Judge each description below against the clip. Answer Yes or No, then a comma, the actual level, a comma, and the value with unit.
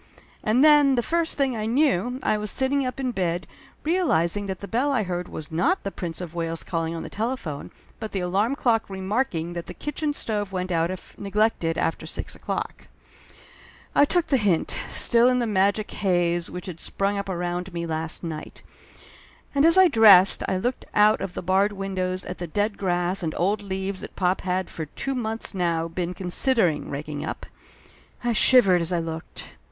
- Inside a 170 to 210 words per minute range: Yes, average, 195 wpm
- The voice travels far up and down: No, average, 5.0 semitones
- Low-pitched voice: No, high, 195 Hz